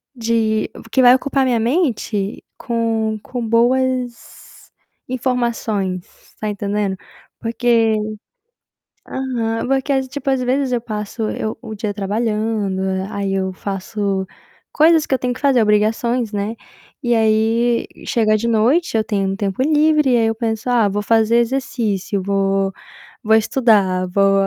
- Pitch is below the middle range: No, high, 225 Hz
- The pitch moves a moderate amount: Yes, average, 3.2 semitones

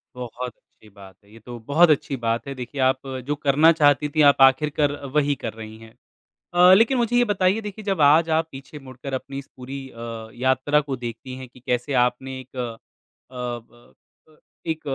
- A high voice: No, low, 135 Hz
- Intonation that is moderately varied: Yes, average, 3.7 semitones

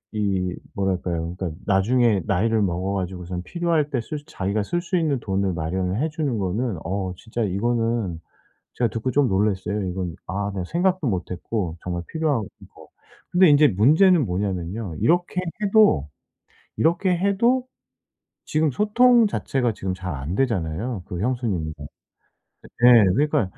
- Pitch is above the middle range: No, low, 105 Hz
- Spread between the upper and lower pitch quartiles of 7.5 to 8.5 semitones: Yes, wide, 8.2 semitones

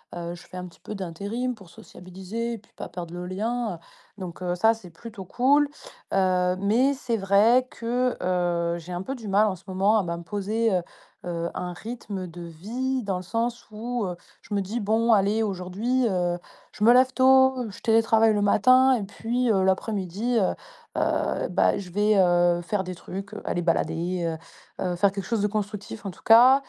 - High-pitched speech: Yes, high, 200 Hz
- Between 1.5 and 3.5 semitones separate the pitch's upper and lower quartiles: No, average, 4.2 semitones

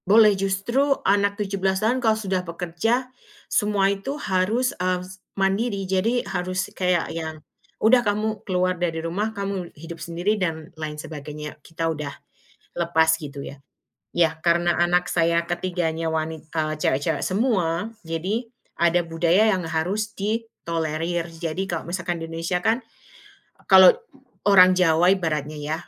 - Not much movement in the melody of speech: No, average, 3.4 semitones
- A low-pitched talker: No, medium, 180 Hz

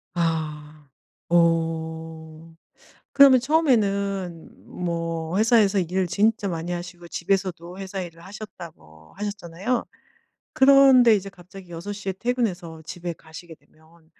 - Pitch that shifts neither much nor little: Yes, average, 3.6 semitones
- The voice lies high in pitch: No, medium, 175 Hz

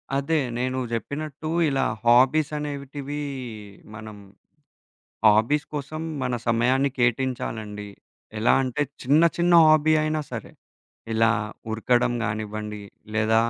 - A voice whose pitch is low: Yes, low, 130 Hz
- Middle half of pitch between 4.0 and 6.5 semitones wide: Yes, average, 4.7 semitones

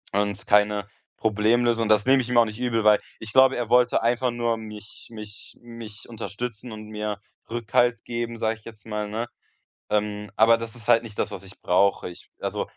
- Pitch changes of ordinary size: No, narrow, 2.1 semitones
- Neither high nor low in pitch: No, low, 110 Hz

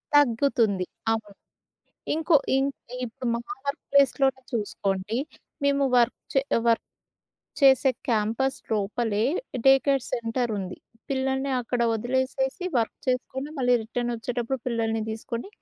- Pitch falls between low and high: No, high, 245 Hz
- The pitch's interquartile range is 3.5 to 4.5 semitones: No, average, 3.1 semitones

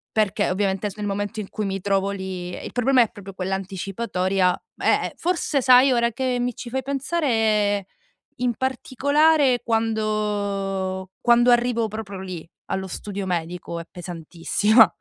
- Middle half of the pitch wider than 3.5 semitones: Yes, average, 4.2 semitones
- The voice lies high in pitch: Yes, high, 210 Hz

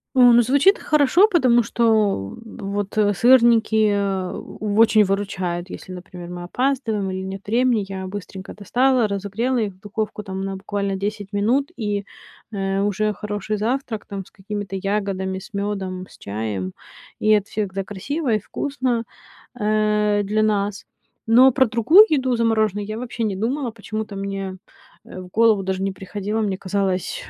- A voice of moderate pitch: No, high, 205 Hz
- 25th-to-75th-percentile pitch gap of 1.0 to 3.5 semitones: Yes, average, 2.9 semitones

